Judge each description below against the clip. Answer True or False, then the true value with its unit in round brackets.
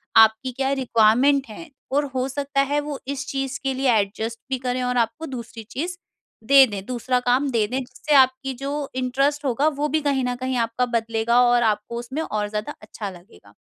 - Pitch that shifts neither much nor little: True (3.2 semitones)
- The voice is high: True (255 Hz)